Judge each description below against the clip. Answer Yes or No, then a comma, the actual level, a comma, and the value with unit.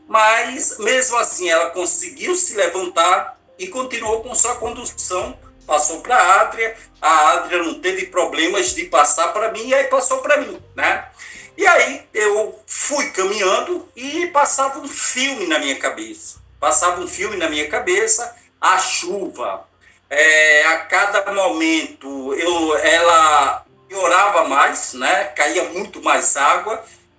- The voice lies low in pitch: No, high, 240 Hz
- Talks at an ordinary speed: Yes, average, 140 wpm